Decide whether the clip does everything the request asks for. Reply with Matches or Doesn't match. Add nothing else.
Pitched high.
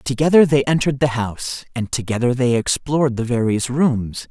Doesn't match